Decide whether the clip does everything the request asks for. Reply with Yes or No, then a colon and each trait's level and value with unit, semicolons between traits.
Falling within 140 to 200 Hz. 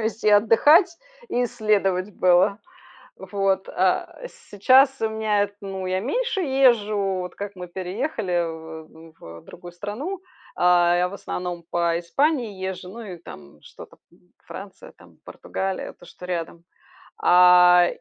Yes: high, 190 Hz